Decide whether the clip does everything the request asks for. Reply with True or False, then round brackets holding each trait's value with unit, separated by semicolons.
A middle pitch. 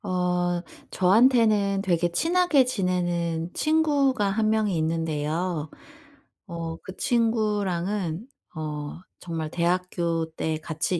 True (180 Hz)